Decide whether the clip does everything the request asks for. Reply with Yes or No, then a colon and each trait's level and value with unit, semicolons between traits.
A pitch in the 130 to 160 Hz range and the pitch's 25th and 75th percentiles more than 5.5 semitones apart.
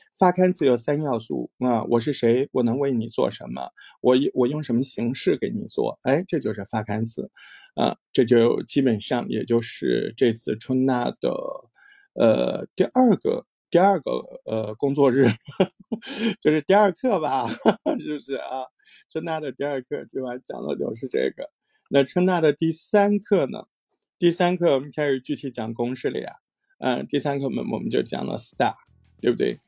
Yes: medium, 140 Hz; wide, 6.4 semitones